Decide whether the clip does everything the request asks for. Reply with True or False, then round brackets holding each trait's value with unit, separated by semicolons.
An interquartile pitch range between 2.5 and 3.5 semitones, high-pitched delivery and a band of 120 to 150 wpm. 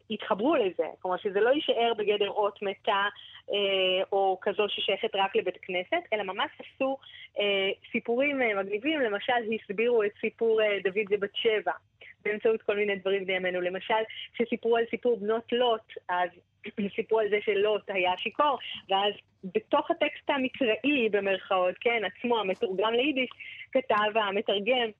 True (3.2 semitones; 215 Hz; 145 wpm)